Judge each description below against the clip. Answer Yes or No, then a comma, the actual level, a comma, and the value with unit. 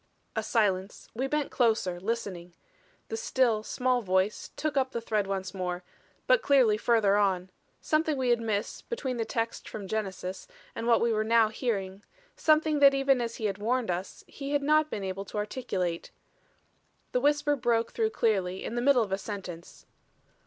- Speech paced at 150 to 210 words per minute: Yes, average, 180 wpm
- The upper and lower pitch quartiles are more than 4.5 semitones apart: Yes, average, 5.1 semitones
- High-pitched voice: Yes, high, 225 Hz